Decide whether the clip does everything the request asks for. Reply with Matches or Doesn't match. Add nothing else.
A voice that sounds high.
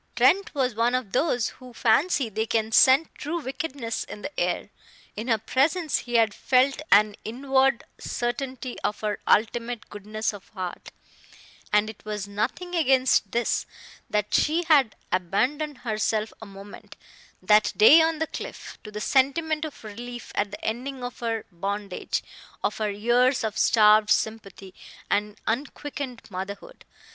Matches